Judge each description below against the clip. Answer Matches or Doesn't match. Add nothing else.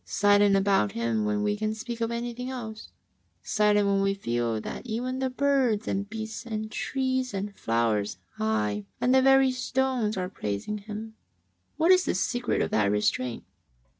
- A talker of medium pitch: Doesn't match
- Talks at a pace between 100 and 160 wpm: Doesn't match